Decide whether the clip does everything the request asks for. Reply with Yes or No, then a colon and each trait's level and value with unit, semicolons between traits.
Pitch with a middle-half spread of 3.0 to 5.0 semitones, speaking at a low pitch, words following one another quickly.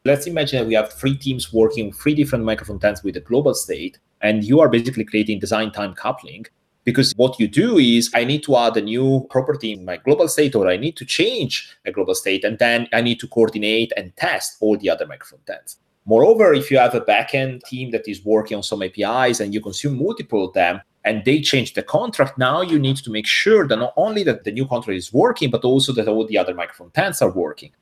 Yes: average, 3.7 semitones; low, 115 Hz; fast, 235 wpm